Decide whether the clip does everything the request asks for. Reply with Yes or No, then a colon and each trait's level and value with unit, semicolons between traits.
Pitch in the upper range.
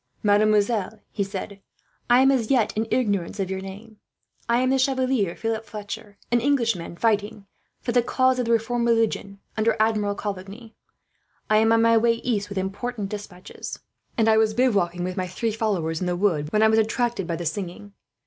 Yes: high, 215 Hz